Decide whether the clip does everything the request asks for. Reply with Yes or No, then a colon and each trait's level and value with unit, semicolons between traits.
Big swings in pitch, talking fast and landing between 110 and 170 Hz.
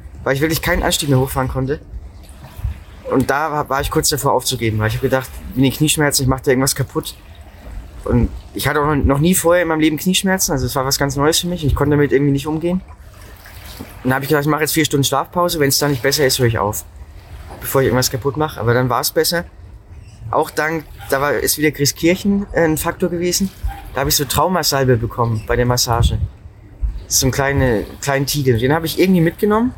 Yes: wide, 6.1 semitones; fast, 225 wpm; low, 135 Hz